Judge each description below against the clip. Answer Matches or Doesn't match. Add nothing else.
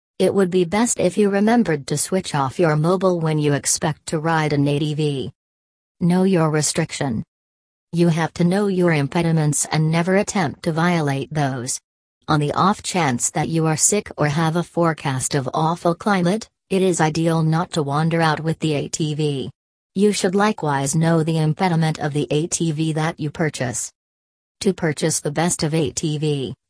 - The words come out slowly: Doesn't match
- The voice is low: Doesn't match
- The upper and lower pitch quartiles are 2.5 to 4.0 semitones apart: Matches